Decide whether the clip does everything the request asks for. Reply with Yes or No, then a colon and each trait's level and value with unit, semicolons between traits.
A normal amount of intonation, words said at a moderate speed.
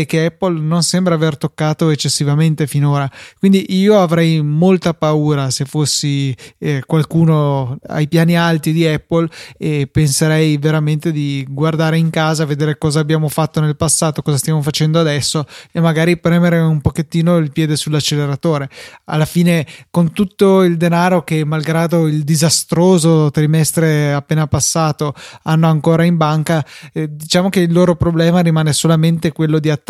No: narrow, 1.7 semitones; average, 150 wpm